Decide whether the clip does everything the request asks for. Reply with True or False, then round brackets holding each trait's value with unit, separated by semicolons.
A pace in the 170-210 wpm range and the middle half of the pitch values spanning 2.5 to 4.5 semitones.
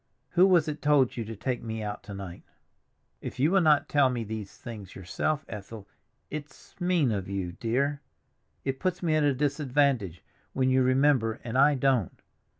False (175 wpm; 5.0 semitones)